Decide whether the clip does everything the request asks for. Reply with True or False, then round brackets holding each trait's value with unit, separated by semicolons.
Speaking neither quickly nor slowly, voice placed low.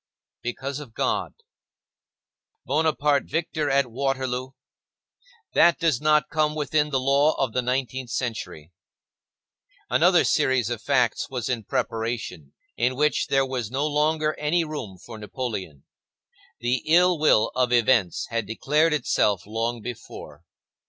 False (130 wpm; 130 Hz)